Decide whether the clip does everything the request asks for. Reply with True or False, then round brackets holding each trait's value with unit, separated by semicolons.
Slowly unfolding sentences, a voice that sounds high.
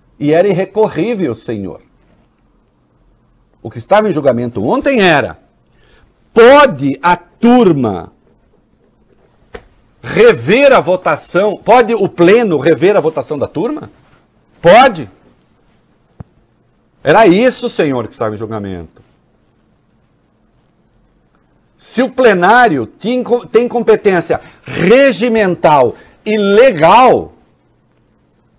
True (90 wpm; 200 Hz)